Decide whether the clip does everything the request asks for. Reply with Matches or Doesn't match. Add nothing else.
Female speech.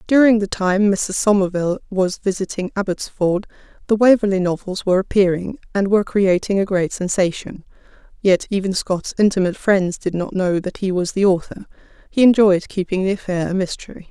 Matches